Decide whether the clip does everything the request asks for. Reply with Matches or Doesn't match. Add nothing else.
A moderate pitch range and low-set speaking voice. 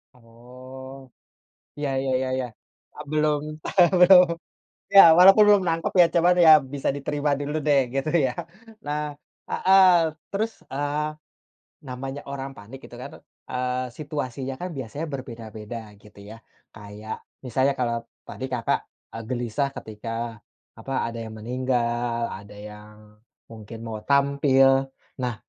Matches